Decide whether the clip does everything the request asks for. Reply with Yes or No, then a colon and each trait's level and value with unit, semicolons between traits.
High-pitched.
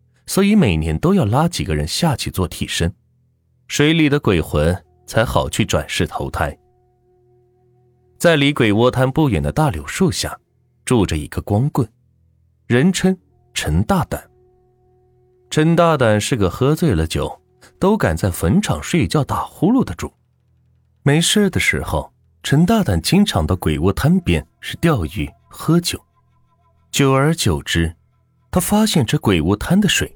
No: low, 120 Hz